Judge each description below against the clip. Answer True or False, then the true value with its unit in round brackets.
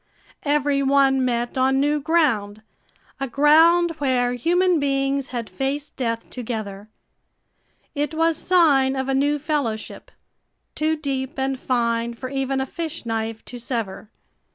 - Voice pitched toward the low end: False (270 Hz)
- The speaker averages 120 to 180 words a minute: True (135 wpm)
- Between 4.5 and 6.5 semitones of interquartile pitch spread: False (3.5 semitones)